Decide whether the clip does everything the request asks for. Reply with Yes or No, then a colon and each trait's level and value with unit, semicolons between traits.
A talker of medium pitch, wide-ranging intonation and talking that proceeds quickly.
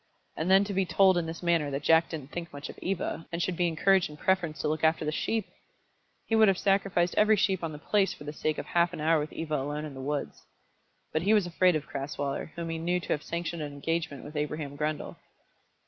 No: medium, 165 Hz; average, 3.2 semitones; fast, 245 wpm